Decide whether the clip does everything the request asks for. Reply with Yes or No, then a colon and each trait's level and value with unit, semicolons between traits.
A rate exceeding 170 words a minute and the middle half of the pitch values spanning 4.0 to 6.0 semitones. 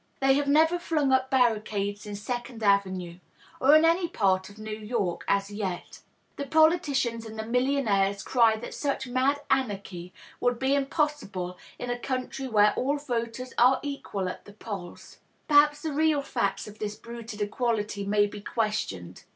No: average, 165 wpm; average, 5.1 semitones